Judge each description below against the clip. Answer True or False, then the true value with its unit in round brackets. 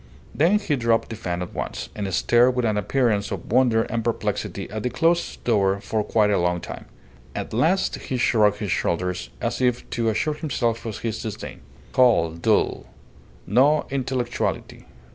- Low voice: True (115 Hz)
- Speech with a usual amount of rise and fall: True (3.7 semitones)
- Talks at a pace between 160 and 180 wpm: True (170 wpm)